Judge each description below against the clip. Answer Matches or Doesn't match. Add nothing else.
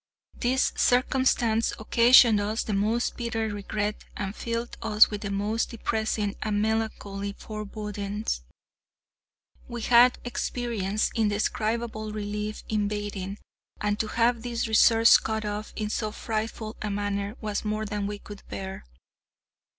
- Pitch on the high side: Matches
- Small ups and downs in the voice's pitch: Matches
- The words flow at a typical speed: Doesn't match